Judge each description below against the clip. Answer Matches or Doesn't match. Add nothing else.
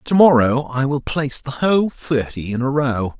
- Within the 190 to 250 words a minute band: Matches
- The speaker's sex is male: Matches